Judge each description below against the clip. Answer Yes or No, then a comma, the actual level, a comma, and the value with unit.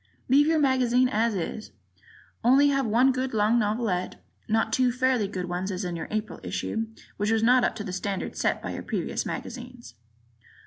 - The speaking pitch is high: Yes, high, 225 Hz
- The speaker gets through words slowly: No, average, 185 wpm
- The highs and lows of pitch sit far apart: No, average, 3.6 semitones